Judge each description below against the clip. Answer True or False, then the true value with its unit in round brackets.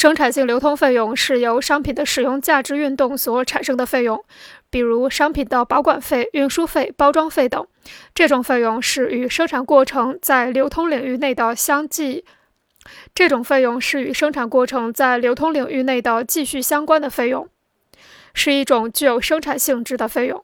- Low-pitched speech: False (270 Hz)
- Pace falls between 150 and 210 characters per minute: False (275 characters per minute)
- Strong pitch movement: False (2.7 semitones)